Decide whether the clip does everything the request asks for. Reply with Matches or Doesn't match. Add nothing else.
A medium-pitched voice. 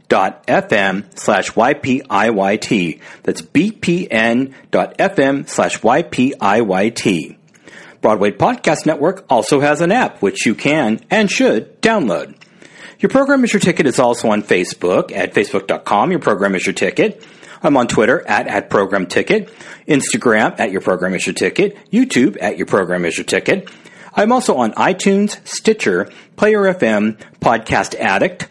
Matches